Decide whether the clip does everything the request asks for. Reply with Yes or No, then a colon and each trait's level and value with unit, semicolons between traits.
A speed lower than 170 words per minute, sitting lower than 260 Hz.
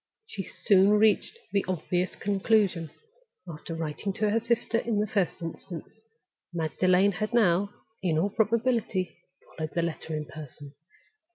Yes: average, 140 wpm; high, 190 Hz